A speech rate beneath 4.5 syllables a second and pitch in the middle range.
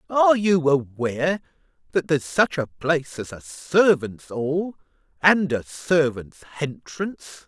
Yes: 4.2 syllables/s; medium, 155 Hz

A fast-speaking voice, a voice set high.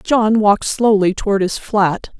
No: average, 165 wpm; high, 205 Hz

